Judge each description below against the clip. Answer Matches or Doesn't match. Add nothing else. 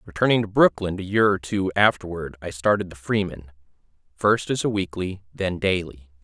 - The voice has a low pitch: Matches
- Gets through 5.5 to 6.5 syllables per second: Doesn't match